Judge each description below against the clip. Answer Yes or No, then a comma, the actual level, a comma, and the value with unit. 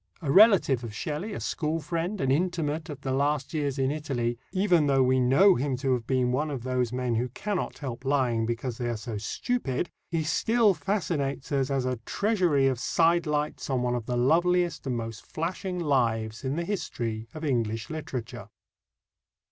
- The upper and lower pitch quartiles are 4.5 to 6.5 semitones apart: Yes, average, 4.9 semitones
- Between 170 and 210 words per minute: Yes, average, 185 wpm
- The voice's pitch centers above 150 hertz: No, medium, 140 Hz